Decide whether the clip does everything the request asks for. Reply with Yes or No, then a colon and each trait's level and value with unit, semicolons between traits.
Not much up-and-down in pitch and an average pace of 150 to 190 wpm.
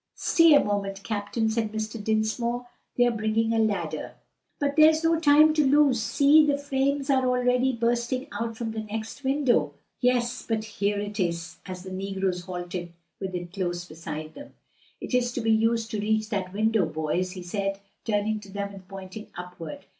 No: average, 4.3 semitones; average, 185 wpm